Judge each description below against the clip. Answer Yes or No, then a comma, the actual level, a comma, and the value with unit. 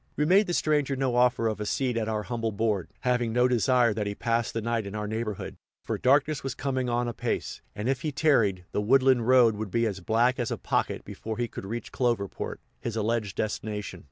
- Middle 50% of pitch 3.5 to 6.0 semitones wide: No, average, 3.0 semitones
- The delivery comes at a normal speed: No, fast, 225 wpm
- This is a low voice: Yes, low, 115 Hz